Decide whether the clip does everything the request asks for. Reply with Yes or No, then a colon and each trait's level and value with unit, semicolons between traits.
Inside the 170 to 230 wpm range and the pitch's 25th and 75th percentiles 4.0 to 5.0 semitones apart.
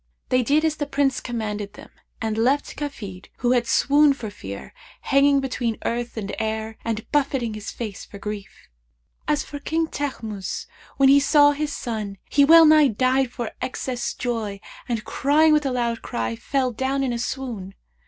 Yes: average, 180 wpm; average, 4.4 semitones